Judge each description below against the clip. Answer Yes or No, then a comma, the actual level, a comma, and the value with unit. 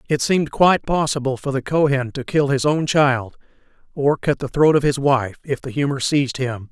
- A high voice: No, medium, 140 Hz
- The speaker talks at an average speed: No, fast, 215 wpm